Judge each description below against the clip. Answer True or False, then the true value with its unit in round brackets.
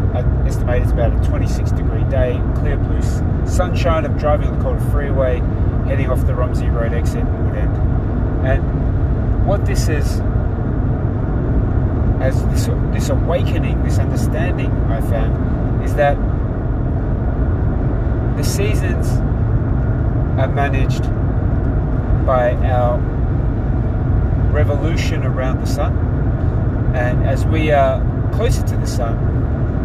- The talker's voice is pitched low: True (115 Hz)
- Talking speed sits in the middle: False (115 wpm)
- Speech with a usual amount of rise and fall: False (2.2 semitones)